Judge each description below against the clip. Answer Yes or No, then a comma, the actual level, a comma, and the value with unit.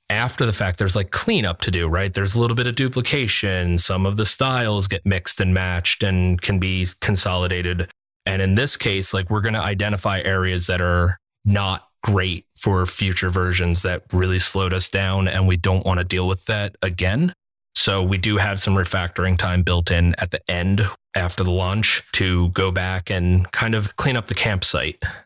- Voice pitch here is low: Yes, very low, 95 Hz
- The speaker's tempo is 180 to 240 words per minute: Yes, average, 195 wpm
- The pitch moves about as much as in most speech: No, narrow, 2.1 semitones